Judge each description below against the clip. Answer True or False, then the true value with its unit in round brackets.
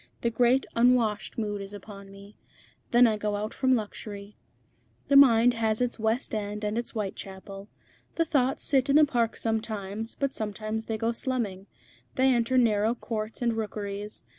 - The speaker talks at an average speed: True (165 wpm)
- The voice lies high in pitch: True (220 Hz)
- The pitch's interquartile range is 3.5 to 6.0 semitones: False (2.7 semitones)